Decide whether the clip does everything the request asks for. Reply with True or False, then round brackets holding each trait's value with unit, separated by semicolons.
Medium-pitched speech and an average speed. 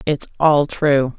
True (145 Hz; 150 wpm)